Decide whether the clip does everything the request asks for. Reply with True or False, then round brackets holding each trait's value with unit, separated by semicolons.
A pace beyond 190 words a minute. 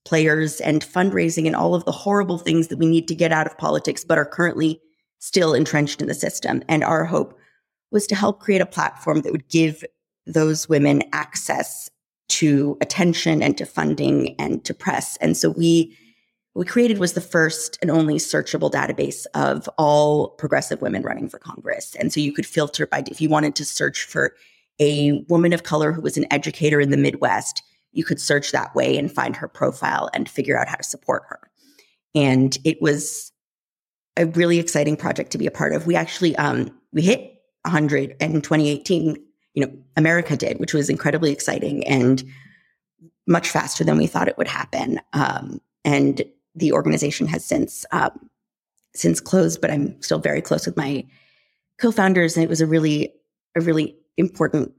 False (185 wpm)